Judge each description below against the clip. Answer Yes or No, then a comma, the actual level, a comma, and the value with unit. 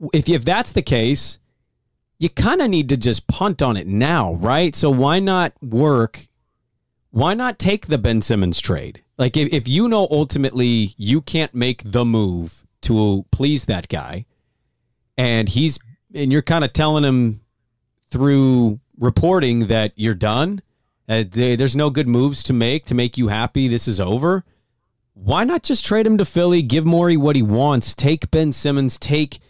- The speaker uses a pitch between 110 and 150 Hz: Yes, low, 135 Hz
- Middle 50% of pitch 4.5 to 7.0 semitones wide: Yes, average, 5.1 semitones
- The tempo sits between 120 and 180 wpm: Yes, average, 175 wpm